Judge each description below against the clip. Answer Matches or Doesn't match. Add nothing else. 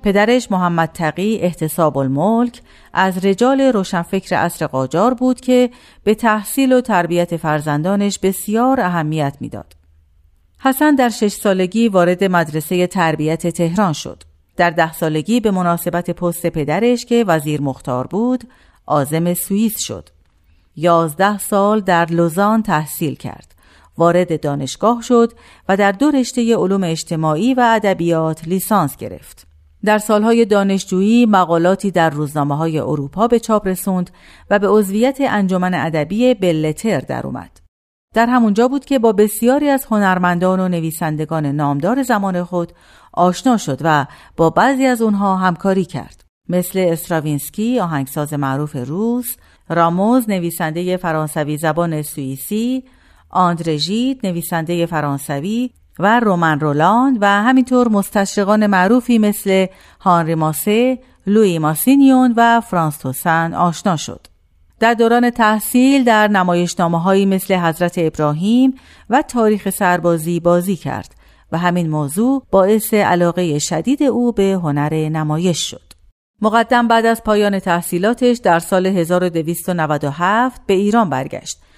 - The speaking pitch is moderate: Matches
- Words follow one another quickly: Doesn't match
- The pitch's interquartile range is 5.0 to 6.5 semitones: Matches